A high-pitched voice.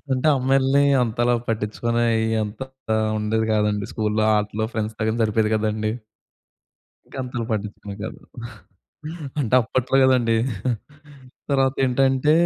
No: low, 115 Hz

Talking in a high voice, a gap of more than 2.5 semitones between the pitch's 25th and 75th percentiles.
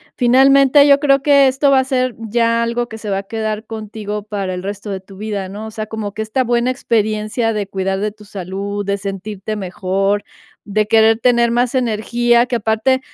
Yes: high, 220 Hz; average, 2.9 semitones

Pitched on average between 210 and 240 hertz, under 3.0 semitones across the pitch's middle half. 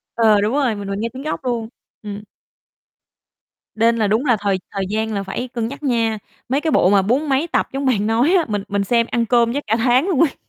No: high, 230 Hz; average, 4.0 semitones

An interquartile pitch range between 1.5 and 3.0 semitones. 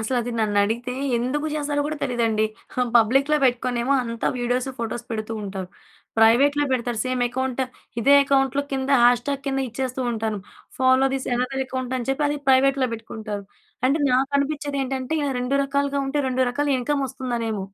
Yes: narrow, 2.6 semitones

